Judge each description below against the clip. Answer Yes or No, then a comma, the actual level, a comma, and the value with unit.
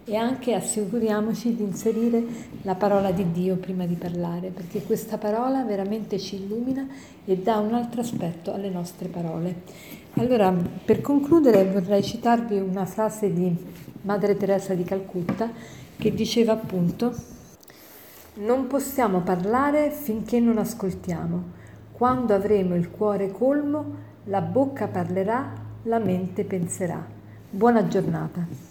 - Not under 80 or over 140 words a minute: Yes, average, 125 wpm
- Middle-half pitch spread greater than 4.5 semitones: No, average, 3.8 semitones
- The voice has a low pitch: No, high, 200 Hz